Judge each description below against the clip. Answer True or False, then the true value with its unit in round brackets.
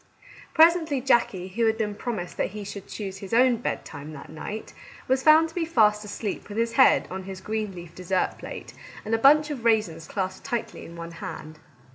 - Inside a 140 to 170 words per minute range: False (200 wpm)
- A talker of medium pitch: False (215 Hz)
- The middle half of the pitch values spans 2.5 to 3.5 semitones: False (4.7 semitones)